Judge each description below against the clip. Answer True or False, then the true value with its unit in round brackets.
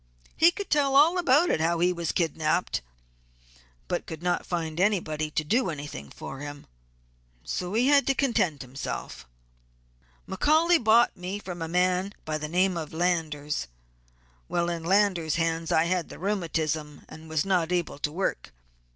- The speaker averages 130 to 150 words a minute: False (160 wpm)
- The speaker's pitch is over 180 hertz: False (175 Hz)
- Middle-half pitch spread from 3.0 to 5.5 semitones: True (4.3 semitones)